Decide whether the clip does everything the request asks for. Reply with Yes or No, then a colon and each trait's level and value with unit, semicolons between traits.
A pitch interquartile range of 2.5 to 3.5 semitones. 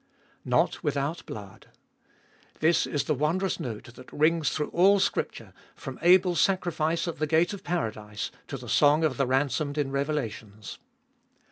No: average, 4.5 semitones